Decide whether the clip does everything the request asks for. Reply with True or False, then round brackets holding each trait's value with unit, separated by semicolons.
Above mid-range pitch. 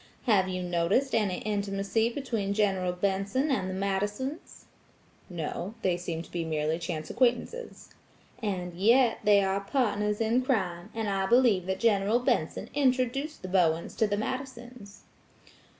True (200 Hz)